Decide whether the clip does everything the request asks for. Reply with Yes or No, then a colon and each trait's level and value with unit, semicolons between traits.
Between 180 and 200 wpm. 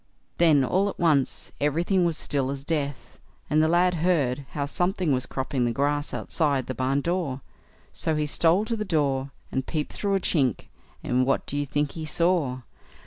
Yes: average, 195 wpm